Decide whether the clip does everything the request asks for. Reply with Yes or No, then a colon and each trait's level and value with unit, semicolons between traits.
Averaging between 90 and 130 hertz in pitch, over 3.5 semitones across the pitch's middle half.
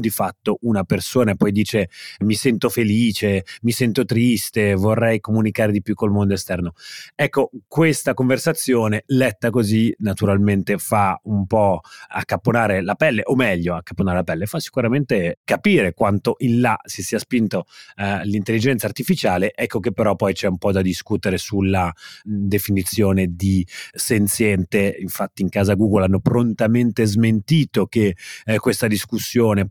No: low, 105 Hz; average, 3.0 semitones